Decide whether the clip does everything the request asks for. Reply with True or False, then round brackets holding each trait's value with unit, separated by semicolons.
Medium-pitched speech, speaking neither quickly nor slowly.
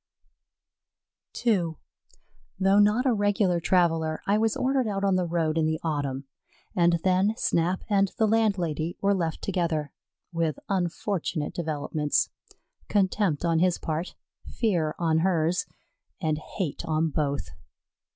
False (175 Hz; 130 wpm)